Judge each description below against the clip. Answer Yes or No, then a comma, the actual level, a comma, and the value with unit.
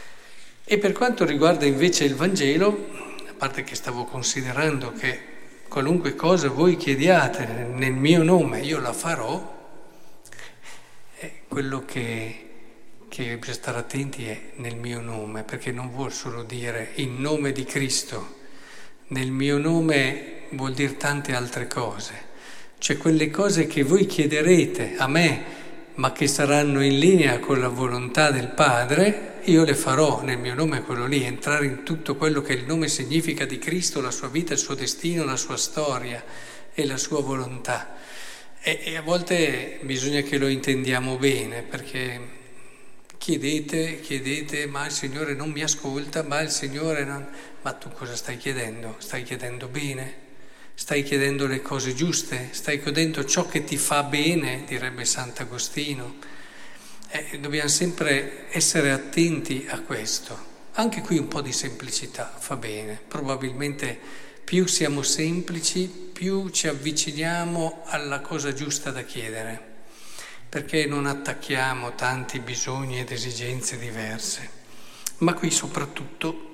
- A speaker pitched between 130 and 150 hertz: Yes, medium, 140 Hz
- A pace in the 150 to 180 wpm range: No, average, 140 wpm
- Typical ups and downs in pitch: Yes, average, 3.6 semitones